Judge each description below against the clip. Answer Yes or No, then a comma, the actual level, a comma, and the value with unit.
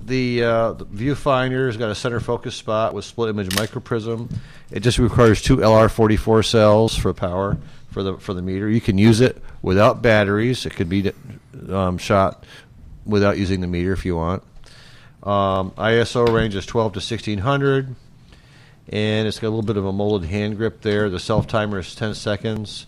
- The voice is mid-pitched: No, low, 110 Hz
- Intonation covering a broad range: No, average, 3.2 semitones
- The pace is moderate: Yes, average, 185 wpm